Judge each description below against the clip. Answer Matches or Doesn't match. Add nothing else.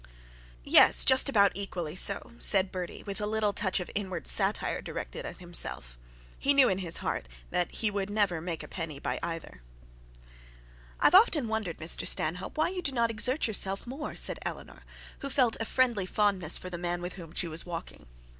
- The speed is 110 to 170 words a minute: Doesn't match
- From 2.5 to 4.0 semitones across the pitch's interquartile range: Doesn't match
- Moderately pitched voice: Doesn't match